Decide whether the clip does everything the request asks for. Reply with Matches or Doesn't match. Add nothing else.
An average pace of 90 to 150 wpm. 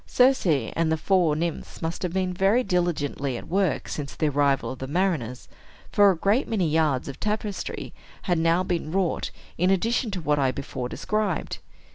Doesn't match